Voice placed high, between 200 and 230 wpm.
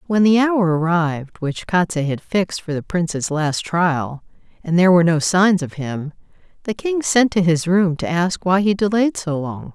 No: medium, 175 Hz; fast, 205 wpm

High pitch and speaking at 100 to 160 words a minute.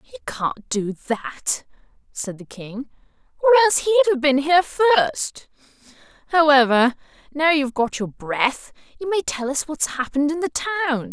Yes: very high, 290 Hz; average, 155 wpm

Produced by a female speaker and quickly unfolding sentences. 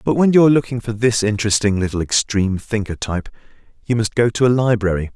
No: male; fast, 210 wpm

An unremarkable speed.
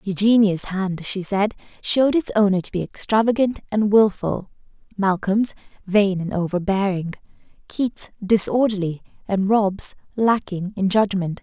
No: slow, 120 wpm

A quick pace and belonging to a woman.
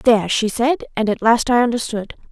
No: average, 180 wpm; female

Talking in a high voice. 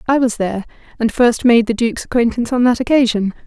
Yes: high, 235 Hz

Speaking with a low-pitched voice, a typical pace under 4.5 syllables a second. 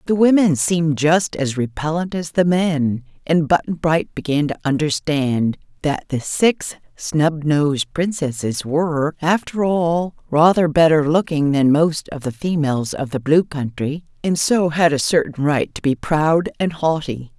No: medium, 155 Hz; 4.3 syllables/s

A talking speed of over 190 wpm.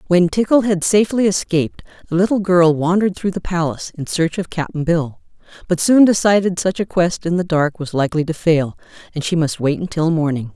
Yes: fast, 205 wpm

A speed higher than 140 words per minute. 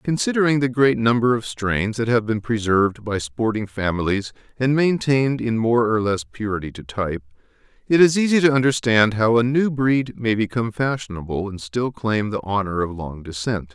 Yes: average, 185 wpm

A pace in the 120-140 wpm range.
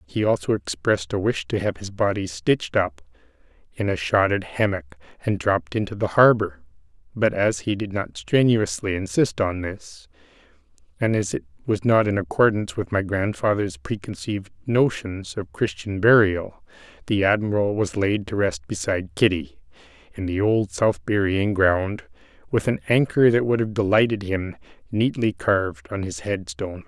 No: average, 160 wpm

